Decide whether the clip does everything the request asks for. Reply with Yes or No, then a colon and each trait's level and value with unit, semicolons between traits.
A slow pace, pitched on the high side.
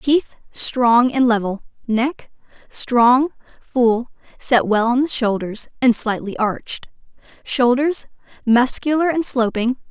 Yes: slow, 95 wpm; high, 245 Hz